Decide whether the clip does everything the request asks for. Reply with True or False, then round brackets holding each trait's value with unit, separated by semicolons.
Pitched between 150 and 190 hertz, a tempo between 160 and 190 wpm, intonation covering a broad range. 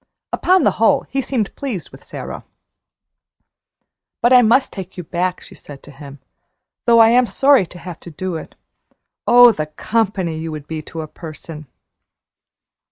True (185 Hz; 165 wpm; 7.2 semitones)